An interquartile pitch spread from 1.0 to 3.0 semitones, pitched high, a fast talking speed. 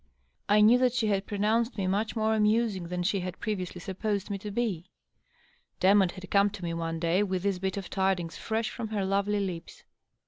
Yes: narrow, 2.6 semitones; high, 200 Hz; fast, 210 wpm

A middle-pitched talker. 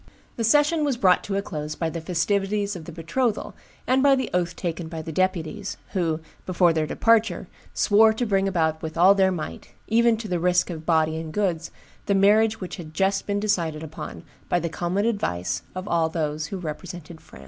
Yes: medium, 180 Hz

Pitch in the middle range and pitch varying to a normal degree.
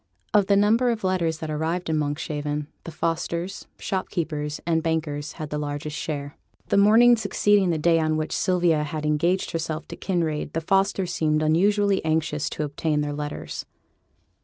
Yes: medium, 160 Hz; average, 3.6 semitones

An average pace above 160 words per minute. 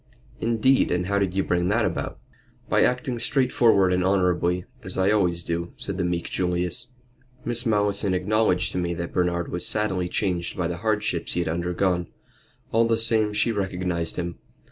Yes: average, 175 wpm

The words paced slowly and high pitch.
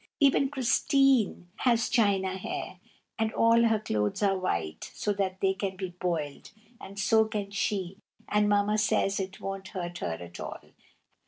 No: average, 155 wpm; high, 195 Hz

